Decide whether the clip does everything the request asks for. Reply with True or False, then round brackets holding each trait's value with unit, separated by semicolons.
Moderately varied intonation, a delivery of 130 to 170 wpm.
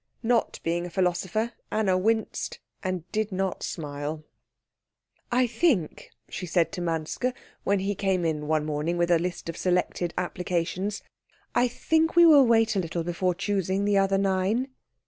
True (4.0 semitones; 160 wpm)